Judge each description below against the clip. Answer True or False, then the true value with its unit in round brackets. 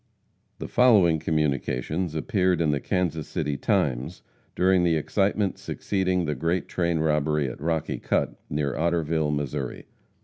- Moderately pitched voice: False (80 Hz)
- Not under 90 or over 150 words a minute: True (135 wpm)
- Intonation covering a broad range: False (3.5 semitones)